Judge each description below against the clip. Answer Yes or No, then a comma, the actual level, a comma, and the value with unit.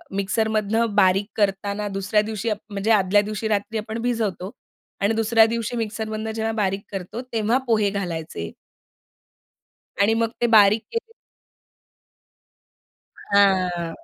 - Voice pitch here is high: Yes, high, 210 Hz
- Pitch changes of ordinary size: No, narrow, 2.2 semitones